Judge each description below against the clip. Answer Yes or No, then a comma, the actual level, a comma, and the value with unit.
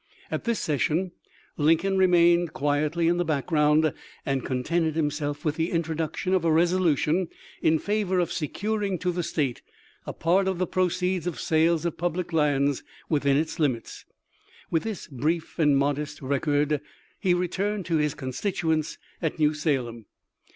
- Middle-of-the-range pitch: Yes, medium, 160 Hz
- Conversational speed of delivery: Yes, average, 160 wpm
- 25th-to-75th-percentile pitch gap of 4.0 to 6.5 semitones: No, average, 3.2 semitones